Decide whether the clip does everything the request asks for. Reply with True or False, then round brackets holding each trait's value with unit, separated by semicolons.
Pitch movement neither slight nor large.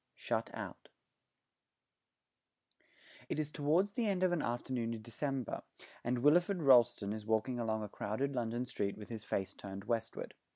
True (5.0 semitones)